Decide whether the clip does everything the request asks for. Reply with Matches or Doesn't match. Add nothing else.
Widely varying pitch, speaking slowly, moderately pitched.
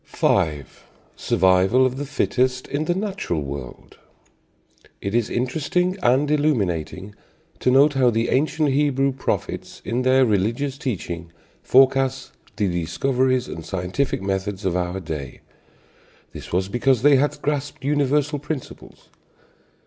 Doesn't match